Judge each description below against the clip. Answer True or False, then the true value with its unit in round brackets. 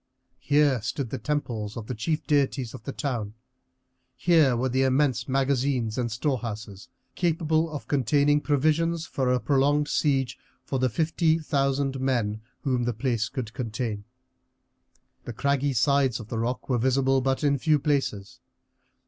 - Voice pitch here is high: False (135 Hz)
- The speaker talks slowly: False (150 wpm)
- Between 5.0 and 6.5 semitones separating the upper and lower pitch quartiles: False (3.4 semitones)